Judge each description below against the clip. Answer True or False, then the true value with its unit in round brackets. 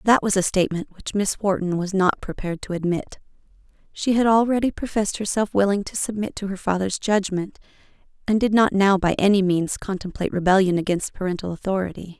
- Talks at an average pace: True (175 wpm)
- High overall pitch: True (195 Hz)